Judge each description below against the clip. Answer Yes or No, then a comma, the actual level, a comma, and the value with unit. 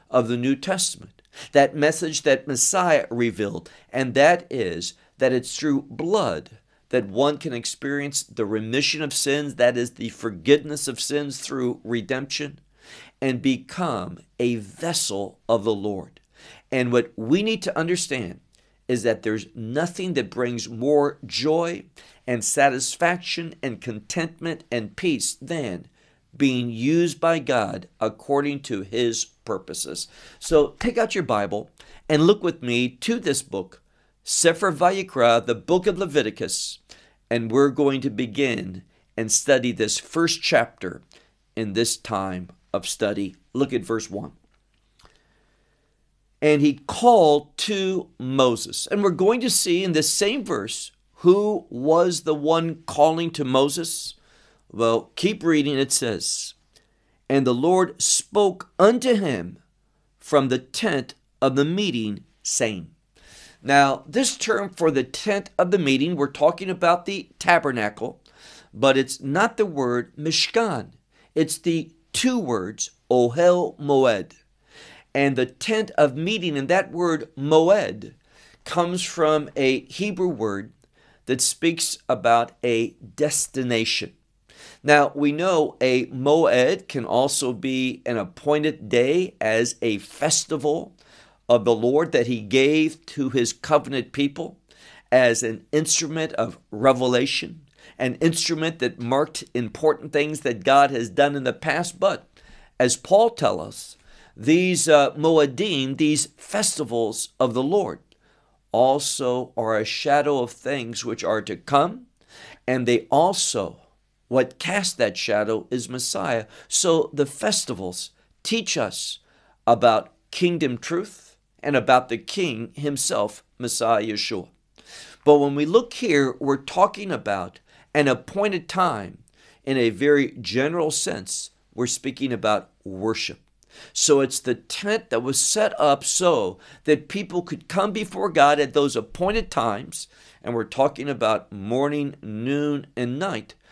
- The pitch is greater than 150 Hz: No, medium, 140 Hz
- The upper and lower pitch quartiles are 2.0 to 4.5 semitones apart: No, average, 5.3 semitones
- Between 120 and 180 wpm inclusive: Yes, slow, 135 wpm